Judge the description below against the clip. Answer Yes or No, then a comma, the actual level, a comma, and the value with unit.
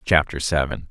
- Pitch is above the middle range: No, very low, 75 Hz